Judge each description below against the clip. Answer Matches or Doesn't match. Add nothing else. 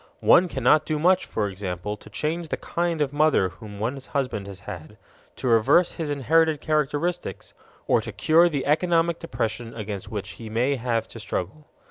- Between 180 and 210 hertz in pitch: Doesn't match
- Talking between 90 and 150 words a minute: Doesn't match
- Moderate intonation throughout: Doesn't match